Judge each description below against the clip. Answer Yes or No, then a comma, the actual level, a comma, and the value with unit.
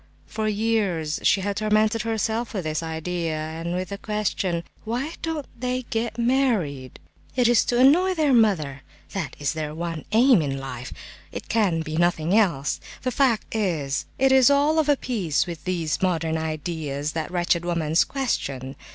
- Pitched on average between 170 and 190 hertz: Yes, medium, 185 Hz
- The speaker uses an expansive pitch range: Yes, wide, 6.7 semitones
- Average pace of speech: Yes, average, 170 wpm